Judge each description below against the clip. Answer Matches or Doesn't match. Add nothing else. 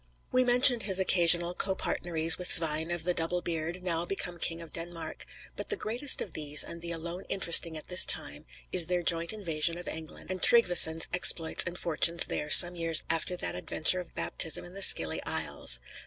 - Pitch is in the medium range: Matches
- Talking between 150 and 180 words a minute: Doesn't match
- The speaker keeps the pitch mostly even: Matches